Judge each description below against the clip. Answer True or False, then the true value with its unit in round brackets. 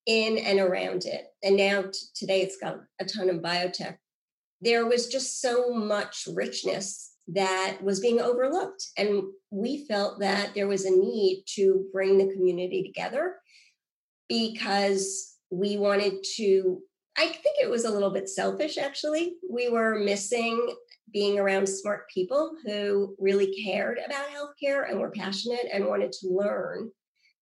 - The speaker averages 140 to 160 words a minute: True (150 wpm)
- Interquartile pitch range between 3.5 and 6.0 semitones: True (3.9 semitones)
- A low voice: False (200 Hz)